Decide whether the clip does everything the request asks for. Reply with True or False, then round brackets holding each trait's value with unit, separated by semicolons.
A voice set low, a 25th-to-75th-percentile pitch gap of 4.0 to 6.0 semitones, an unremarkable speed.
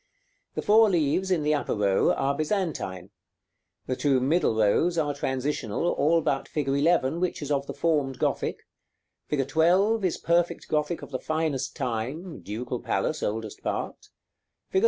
False (150 Hz; 4.5 semitones; 155 wpm)